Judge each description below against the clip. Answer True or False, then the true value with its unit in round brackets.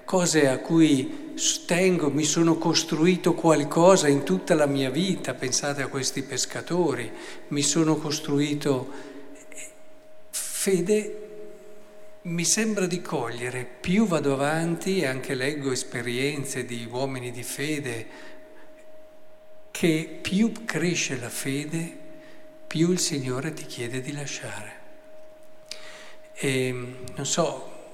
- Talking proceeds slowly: True (110 wpm)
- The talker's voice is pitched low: False (165 Hz)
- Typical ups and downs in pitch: False (7.0 semitones)